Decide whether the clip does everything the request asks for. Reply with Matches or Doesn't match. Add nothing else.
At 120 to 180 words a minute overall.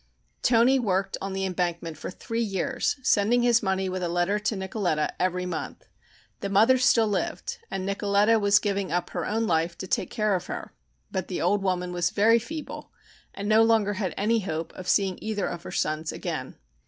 Doesn't match